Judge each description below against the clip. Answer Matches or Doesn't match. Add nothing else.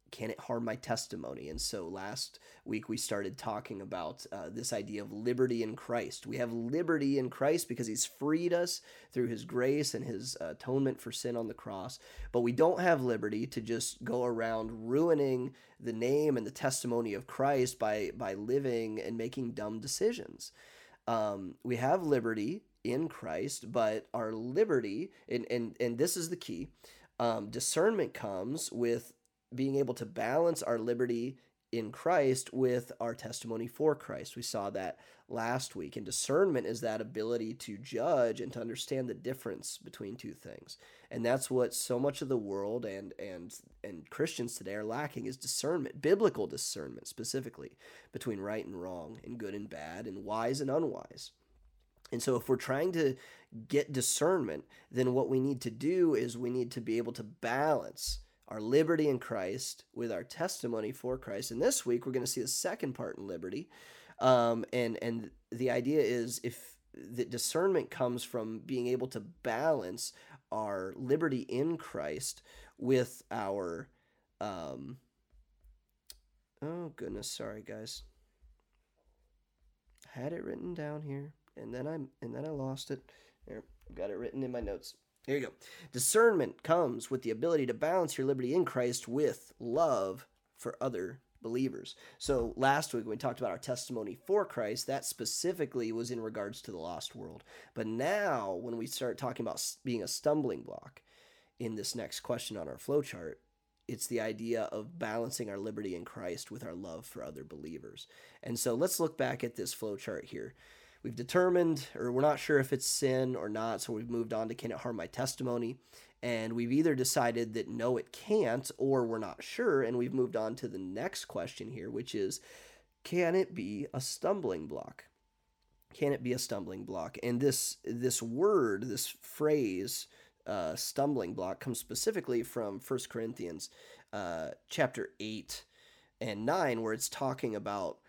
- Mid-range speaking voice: Doesn't match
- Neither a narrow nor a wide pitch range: Matches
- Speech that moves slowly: Doesn't match